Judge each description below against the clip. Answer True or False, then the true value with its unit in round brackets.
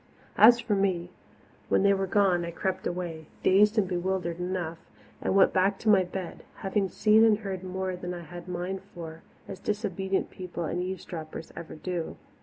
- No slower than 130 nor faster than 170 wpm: False (185 wpm)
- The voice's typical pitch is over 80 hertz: True (185 Hz)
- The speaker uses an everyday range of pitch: False (1.9 semitones)